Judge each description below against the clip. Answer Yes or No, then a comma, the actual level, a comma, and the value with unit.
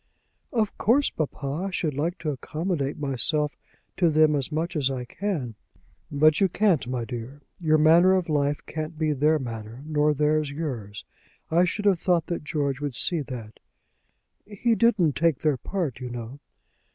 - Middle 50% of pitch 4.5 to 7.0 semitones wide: No, average, 3.8 semitones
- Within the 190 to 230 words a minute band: No, average, 165 wpm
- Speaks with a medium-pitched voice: Yes, medium, 150 Hz